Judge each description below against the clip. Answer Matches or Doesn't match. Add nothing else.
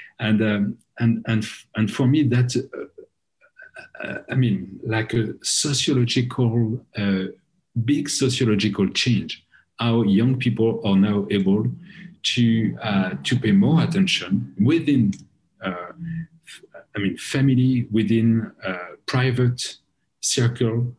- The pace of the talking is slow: Matches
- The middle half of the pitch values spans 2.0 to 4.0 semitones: Doesn't match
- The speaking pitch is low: Matches